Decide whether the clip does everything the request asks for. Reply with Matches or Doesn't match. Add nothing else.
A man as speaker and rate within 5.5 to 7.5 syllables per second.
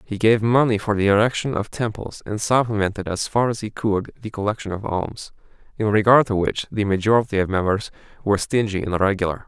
Matches